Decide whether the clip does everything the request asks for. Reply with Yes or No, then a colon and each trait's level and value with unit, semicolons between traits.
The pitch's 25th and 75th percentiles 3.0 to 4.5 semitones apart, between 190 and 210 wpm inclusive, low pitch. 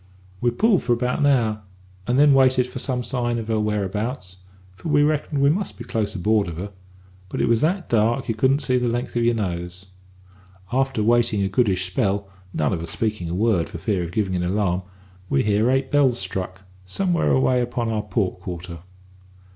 No: average, 5.0 semitones; fast, 205 wpm; low, 110 Hz